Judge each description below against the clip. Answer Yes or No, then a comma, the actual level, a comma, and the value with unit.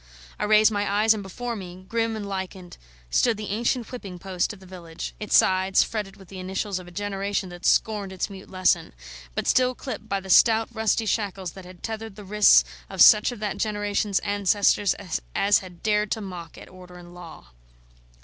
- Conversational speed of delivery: Yes, average, 195 wpm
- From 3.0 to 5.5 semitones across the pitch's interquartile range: No, narrow, 2.5 semitones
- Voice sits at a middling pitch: No, high, 200 Hz